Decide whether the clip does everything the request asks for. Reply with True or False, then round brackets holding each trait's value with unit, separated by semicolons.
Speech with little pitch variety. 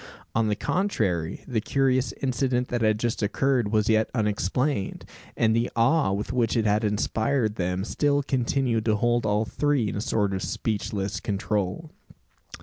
False (3.5 semitones)